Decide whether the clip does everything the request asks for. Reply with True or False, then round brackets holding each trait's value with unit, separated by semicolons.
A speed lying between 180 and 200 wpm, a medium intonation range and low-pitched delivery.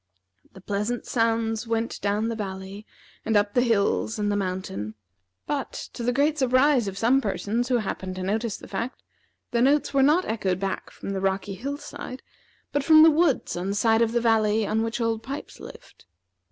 False (195 wpm; 3.8 semitones; 225 Hz)